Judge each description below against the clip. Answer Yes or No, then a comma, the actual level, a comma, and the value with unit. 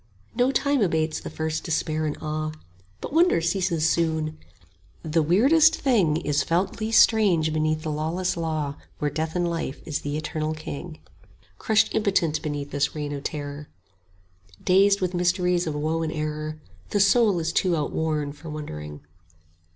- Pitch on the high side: No, medium, 160 Hz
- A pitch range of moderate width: Yes, average, 3.0 semitones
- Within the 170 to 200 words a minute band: No, average, 160 wpm